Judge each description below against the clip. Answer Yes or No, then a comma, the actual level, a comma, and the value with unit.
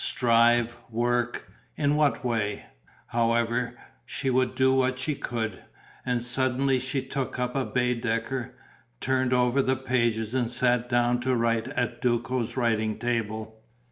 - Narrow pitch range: Yes, narrow, 1.8 semitones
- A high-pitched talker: No, low, 120 Hz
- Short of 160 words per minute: Yes, average, 140 wpm